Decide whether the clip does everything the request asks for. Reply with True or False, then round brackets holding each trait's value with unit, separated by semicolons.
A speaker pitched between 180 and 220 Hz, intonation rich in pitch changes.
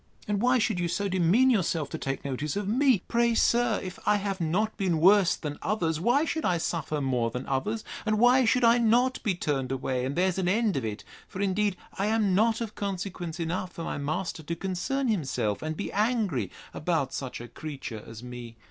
True (185 Hz; 6.3 semitones)